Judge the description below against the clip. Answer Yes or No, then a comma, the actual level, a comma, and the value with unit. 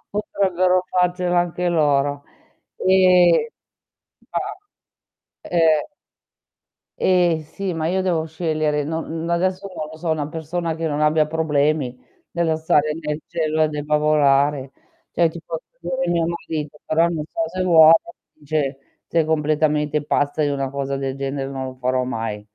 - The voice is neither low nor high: Yes, medium, 155 Hz